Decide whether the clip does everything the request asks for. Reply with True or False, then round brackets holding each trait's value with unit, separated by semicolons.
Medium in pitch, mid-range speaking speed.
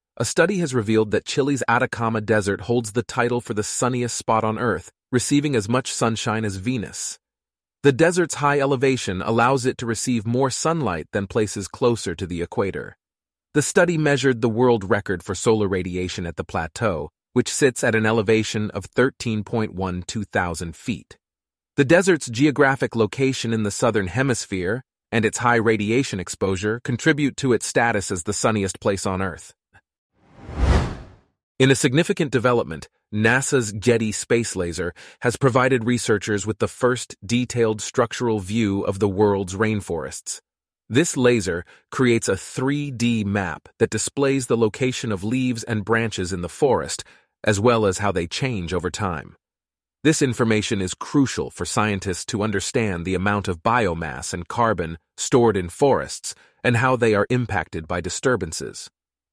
False (115 Hz; 155 wpm)